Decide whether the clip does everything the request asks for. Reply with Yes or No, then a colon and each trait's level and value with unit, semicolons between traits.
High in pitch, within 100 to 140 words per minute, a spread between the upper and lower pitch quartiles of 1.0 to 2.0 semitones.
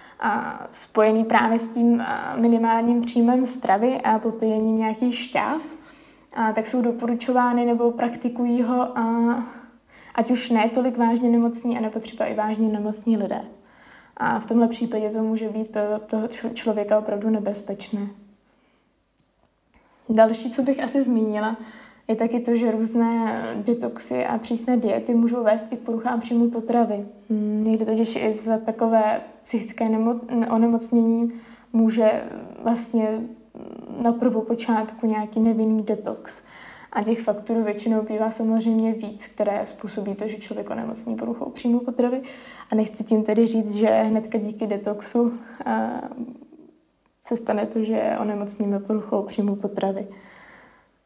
Yes: high, 225 Hz; average, 130 wpm; narrow, 1.7 semitones